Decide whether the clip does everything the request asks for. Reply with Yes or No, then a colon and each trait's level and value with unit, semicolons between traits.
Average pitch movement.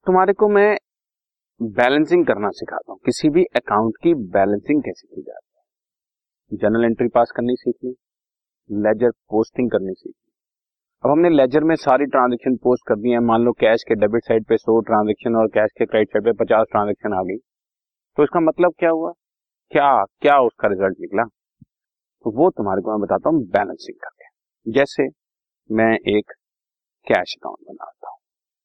No: wide, 6.6 semitones